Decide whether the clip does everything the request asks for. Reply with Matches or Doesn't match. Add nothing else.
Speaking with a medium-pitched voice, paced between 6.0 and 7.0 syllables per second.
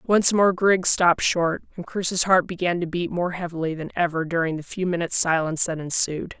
Doesn't match